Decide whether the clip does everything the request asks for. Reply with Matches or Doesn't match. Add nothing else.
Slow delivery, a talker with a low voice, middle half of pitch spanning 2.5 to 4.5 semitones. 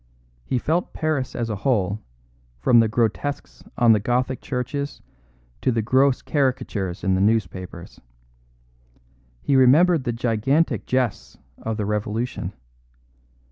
Matches